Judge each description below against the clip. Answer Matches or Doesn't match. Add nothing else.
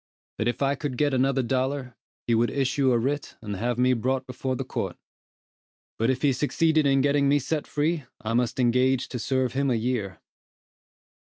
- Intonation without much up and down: Matches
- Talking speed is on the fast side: Doesn't match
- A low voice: Matches